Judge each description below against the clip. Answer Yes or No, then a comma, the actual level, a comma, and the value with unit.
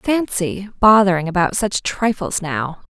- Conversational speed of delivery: No, slow, 125 wpm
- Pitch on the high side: Yes, high, 205 Hz